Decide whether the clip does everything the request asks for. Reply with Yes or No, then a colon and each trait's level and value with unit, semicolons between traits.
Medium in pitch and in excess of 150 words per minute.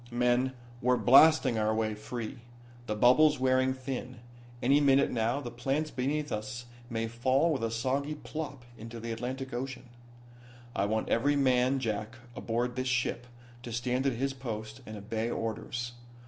No: low, 125 Hz; average, 160 wpm